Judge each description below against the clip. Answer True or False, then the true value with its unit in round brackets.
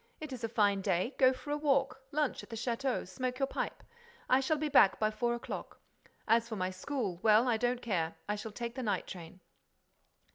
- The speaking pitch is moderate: False (235 Hz)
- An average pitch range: True (4.2 semitones)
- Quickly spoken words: True (215 wpm)